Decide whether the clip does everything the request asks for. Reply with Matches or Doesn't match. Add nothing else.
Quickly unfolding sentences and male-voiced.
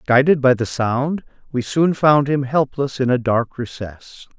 Doesn't match